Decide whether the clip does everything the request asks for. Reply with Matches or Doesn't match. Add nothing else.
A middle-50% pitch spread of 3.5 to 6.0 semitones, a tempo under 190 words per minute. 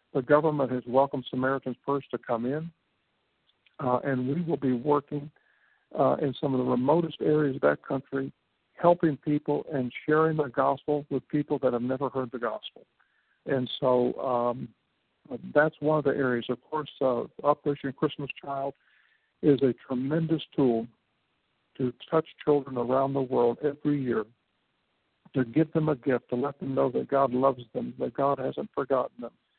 Doesn't match